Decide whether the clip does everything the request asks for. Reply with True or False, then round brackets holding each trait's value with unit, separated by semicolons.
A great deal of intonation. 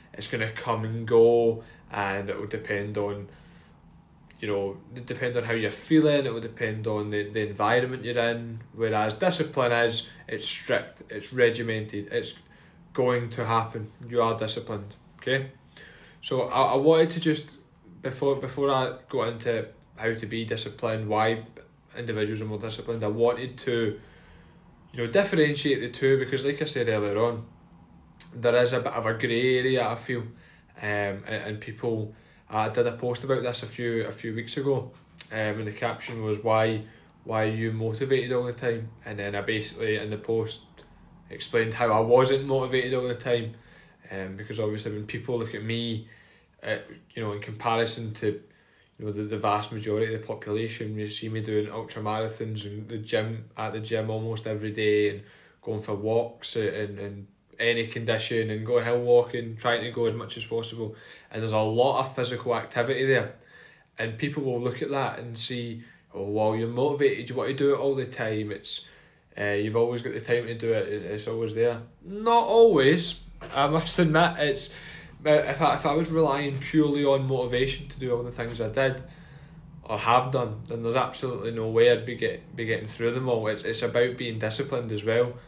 False (2.8 semitones)